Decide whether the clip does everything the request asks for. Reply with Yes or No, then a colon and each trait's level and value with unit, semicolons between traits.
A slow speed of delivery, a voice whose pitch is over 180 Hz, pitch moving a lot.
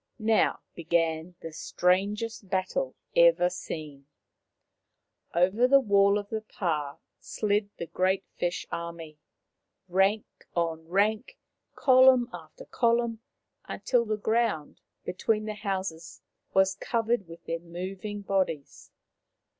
No: slow, 110 wpm; high, 190 Hz; average, 4.4 semitones